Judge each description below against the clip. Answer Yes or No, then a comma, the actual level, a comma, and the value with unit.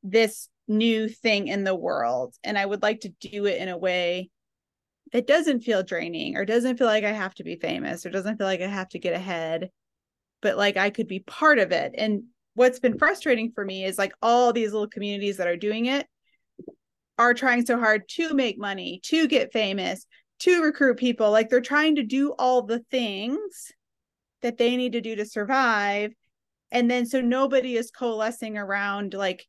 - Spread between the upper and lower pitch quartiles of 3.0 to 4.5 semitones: Yes, average, 3.8 semitones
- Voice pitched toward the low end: No, high, 225 Hz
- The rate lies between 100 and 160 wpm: No, average, 200 wpm